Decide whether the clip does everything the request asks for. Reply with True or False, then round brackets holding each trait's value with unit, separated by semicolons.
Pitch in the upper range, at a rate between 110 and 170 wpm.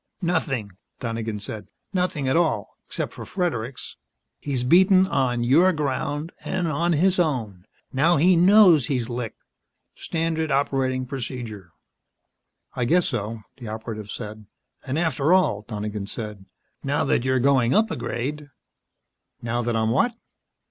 False (130 Hz; 145 wpm)